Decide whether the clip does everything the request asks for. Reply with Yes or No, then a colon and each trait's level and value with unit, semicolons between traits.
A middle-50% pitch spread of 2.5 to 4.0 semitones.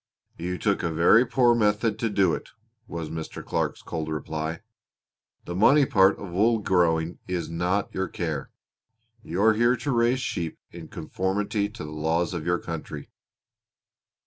No: average, 4.6 semitones